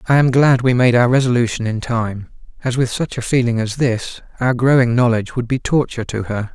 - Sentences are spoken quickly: Yes, fast, 220 wpm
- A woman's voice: No, male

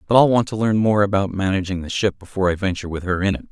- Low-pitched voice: Yes, low, 100 Hz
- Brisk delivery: Yes, fast, 290 wpm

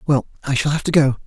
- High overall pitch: No, medium, 145 Hz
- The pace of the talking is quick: Yes, fast, 240 wpm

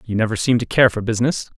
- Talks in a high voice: No, low, 115 Hz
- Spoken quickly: Yes, fast, 265 wpm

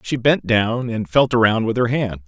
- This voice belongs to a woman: No, male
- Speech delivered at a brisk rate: Yes, fast, 235 wpm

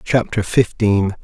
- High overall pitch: No, low, 105 Hz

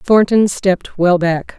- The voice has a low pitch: No, medium, 185 Hz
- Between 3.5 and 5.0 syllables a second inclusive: Yes, 4.0 syllables/s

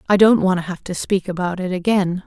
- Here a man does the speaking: No, female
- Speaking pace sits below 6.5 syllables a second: Yes, 5.7 syllables/s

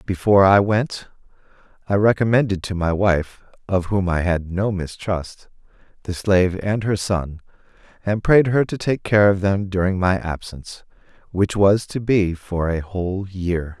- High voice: No, very low, 95 Hz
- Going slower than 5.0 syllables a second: Yes, 4.5 syllables/s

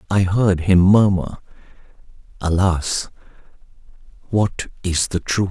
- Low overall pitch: Yes, very low, 95 Hz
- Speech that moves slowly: Yes, slow, 100 wpm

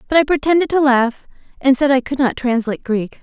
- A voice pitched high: Yes, very high, 265 Hz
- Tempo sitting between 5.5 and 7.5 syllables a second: Yes, 5.9 syllables/s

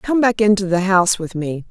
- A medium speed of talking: No, fast, 245 wpm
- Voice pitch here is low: No, high, 195 Hz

